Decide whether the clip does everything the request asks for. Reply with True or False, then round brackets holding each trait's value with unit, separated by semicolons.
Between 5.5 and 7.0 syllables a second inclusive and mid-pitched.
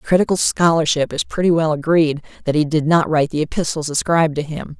True (6.1 syllables/s; 155 Hz)